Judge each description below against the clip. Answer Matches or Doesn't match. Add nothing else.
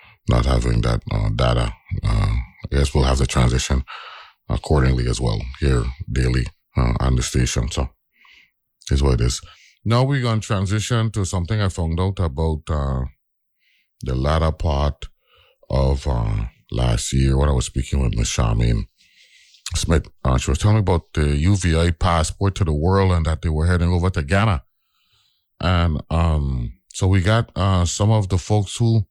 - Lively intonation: Matches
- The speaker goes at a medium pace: Matches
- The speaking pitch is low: Matches